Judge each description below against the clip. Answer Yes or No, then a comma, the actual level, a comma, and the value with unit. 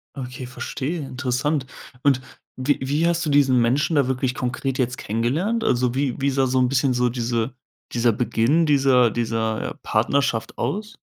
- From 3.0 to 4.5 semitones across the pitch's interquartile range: No, narrow, 2.6 semitones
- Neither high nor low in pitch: No, low, 130 Hz